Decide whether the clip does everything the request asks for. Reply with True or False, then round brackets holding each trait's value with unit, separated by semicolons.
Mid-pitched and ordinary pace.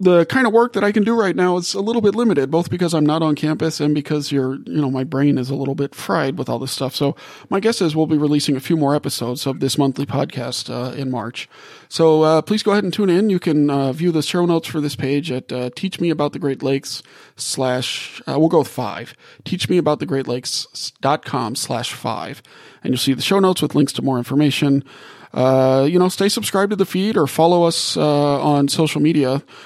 False (150 Hz; 250 wpm)